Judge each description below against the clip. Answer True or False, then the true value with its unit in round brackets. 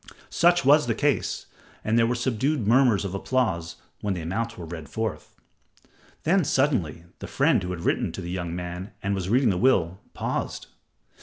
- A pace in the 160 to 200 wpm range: True (180 wpm)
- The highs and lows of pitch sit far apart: True (6.6 semitones)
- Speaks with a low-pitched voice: True (105 Hz)